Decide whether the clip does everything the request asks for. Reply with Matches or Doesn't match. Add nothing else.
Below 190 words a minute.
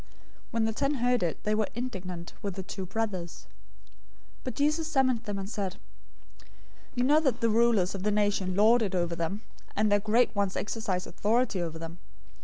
Doesn't match